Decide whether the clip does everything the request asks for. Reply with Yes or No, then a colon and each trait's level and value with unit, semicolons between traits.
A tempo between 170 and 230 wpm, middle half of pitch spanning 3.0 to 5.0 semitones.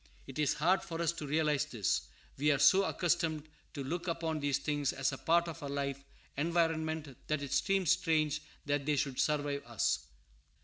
No: average, 185 wpm; narrow, 2.5 semitones